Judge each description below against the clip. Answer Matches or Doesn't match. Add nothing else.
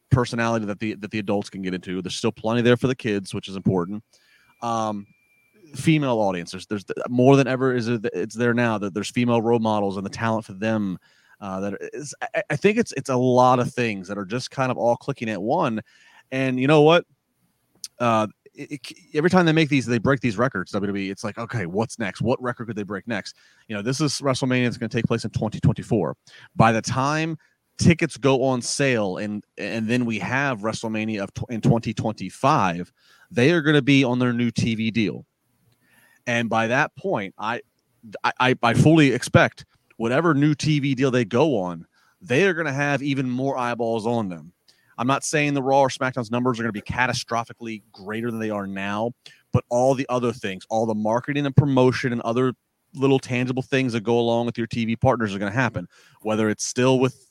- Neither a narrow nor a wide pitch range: Matches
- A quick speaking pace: Matches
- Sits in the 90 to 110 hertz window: Doesn't match